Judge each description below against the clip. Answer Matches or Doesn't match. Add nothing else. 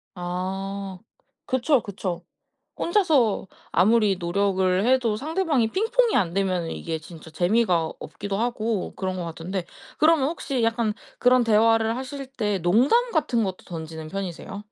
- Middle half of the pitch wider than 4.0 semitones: Matches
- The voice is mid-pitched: Doesn't match